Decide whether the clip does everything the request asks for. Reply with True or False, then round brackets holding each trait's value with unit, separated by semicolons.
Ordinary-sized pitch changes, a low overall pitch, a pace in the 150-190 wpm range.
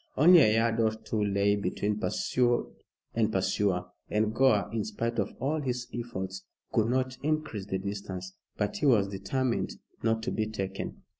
True (3.4 semitones; 110 Hz; 165 wpm)